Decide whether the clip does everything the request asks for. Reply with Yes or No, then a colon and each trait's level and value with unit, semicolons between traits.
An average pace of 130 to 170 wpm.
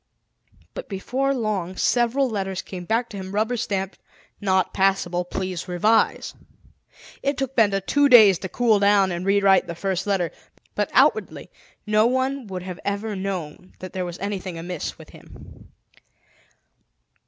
Yes: average, 150 wpm